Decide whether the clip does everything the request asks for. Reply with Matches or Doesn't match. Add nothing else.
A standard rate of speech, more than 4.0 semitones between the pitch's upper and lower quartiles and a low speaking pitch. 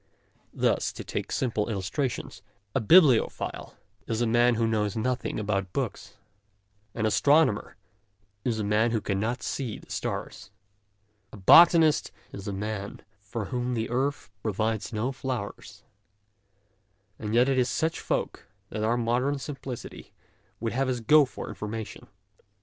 Doesn't match